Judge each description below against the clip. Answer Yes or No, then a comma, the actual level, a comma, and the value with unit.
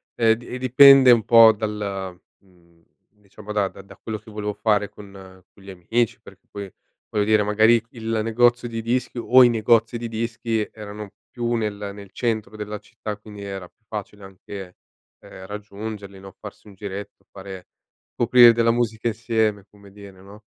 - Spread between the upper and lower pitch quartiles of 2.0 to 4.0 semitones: Yes, narrow, 2.4 semitones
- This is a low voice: Yes, low, 105 Hz